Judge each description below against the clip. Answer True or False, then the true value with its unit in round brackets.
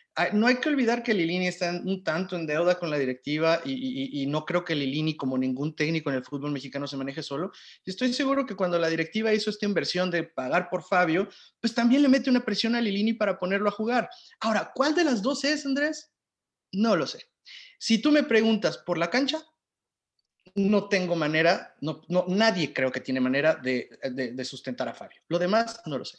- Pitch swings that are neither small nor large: False (7.0 semitones)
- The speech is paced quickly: True (215 wpm)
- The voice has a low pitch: False (180 Hz)